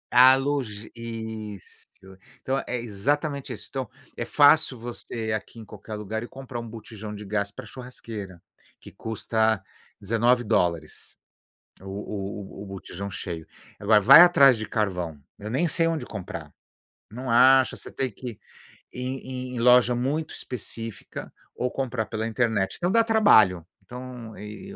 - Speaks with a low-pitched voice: Yes, low, 115 Hz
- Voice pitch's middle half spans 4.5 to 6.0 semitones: No, average, 3.6 semitones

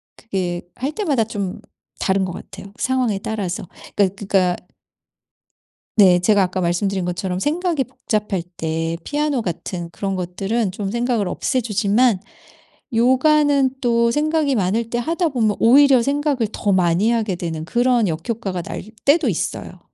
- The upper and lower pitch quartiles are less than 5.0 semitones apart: No, wide, 5.6 semitones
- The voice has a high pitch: Yes, high, 215 Hz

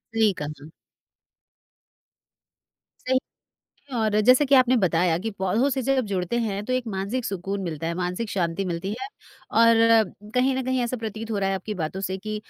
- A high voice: Yes, high, 210 Hz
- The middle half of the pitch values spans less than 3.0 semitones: No, wide, 5.4 semitones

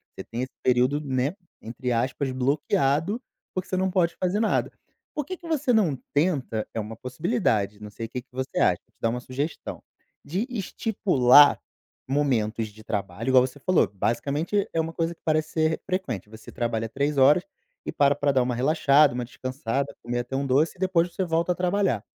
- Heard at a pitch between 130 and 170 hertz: Yes, medium, 140 Hz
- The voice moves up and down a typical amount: No, wide, 5.7 semitones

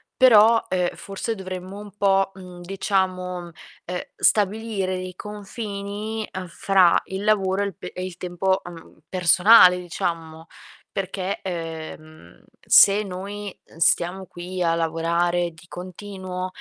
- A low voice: No, medium, 185 Hz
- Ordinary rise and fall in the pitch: No, narrow, 2.2 semitones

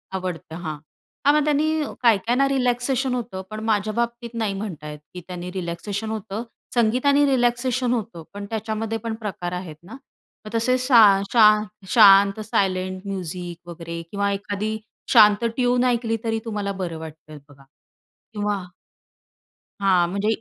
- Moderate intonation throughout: Yes, average, 4.2 semitones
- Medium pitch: No, high, 210 Hz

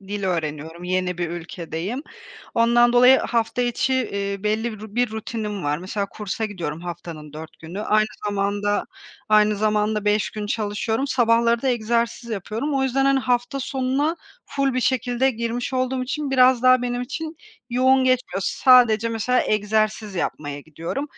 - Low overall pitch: No, high, 220 Hz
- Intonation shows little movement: No, average, 4.0 semitones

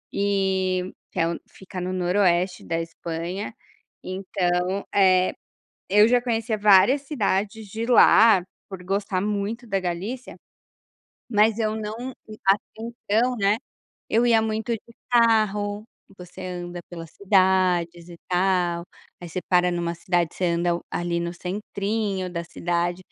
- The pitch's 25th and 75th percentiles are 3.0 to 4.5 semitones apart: Yes, average, 3.3 semitones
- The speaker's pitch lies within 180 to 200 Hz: Yes, high, 190 Hz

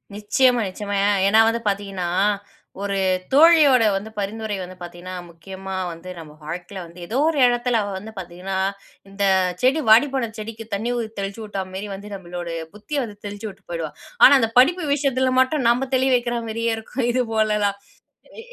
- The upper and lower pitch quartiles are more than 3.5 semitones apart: Yes, average, 4.3 semitones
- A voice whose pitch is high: Yes, high, 210 Hz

